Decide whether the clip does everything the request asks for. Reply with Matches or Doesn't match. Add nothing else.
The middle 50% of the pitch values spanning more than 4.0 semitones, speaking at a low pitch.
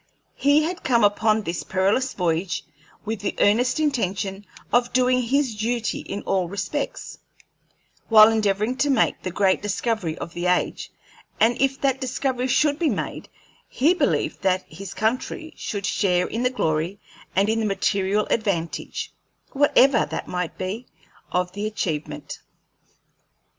Doesn't match